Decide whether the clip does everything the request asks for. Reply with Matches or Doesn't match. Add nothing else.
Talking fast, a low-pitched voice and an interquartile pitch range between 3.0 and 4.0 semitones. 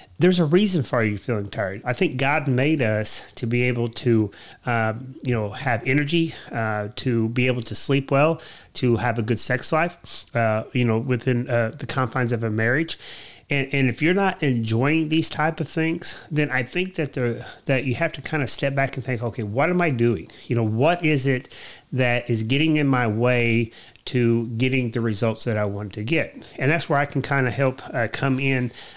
Matches